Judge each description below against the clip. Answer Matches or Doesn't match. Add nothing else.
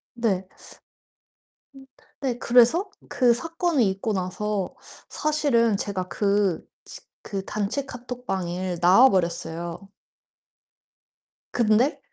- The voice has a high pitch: Matches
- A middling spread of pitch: Matches